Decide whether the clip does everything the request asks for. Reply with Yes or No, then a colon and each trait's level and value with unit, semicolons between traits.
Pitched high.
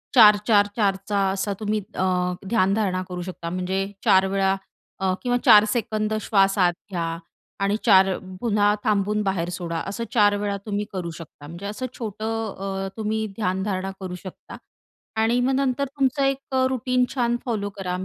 Yes: high, 205 Hz